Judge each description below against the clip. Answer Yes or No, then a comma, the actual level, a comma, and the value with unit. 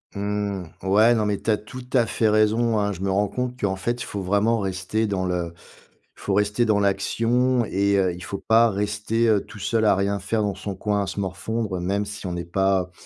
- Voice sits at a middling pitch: No, low, 100 Hz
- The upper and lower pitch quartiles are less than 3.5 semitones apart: Yes, narrow, 2.4 semitones